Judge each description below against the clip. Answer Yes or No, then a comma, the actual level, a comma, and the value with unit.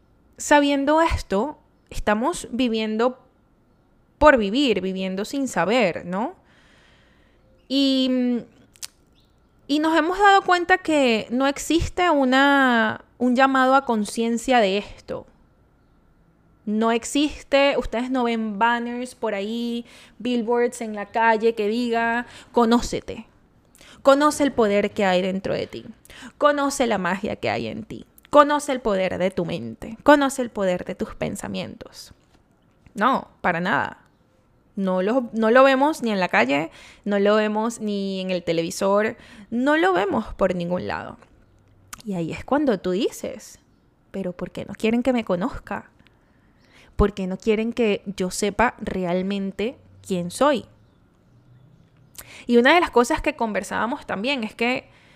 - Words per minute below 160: Yes, average, 140 wpm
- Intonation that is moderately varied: Yes, average, 4.9 semitones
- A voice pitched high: Yes, high, 230 Hz